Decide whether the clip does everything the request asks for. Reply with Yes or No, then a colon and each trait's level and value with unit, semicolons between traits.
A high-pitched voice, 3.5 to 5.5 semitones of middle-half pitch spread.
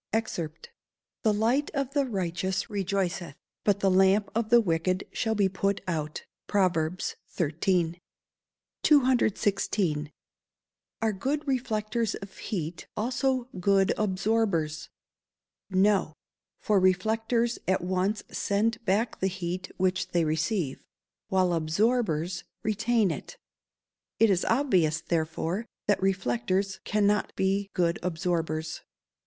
Yes: high, 195 Hz; average, 3.9 semitones